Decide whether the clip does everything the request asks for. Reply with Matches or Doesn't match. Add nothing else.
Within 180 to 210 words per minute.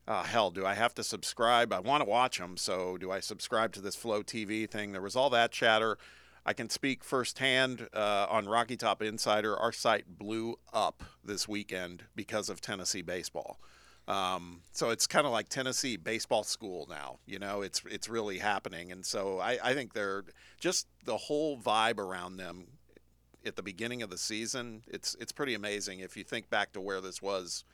Matches